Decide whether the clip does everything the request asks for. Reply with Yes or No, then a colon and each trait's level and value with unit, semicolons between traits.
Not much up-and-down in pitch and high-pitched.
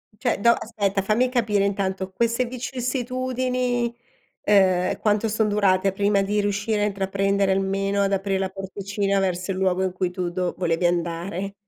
Yes: narrow, 2.2 semitones; high, 200 Hz